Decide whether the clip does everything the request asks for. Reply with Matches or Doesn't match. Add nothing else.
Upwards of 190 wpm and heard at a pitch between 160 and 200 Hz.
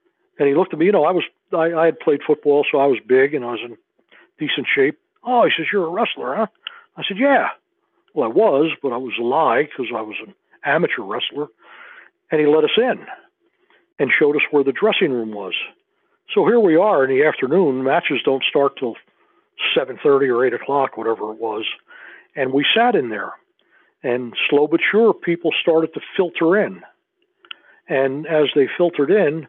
Matches